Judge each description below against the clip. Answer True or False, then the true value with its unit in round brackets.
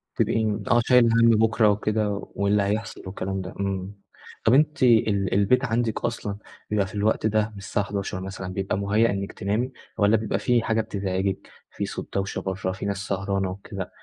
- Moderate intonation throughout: False (2.3 semitones)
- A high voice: False (100 Hz)